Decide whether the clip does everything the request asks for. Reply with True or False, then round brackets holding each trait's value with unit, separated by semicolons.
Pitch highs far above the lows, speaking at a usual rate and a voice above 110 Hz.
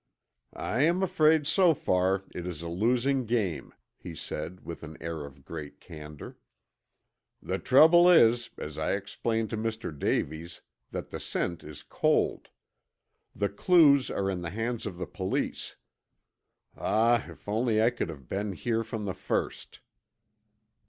False (6.1 semitones; 150 wpm; 105 Hz)